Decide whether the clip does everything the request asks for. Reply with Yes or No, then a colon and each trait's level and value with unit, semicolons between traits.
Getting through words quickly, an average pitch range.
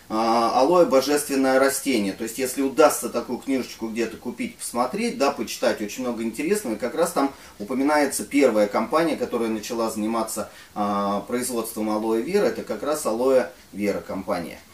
No: average, 145 wpm; average, 3.5 semitones